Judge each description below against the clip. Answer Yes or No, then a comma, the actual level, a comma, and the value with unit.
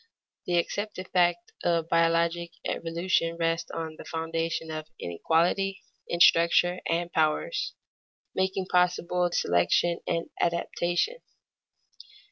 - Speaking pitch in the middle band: Yes, medium, 170 Hz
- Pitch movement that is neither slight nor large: No, narrow, 1.3 semitones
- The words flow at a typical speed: No, slow, 100 wpm